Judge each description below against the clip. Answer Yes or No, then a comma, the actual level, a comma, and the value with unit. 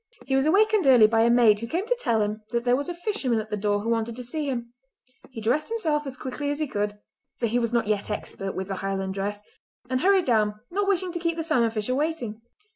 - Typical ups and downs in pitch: No, wide, 6.3 semitones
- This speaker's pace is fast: Yes, fast, 245 wpm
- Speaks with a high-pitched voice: Yes, high, 240 Hz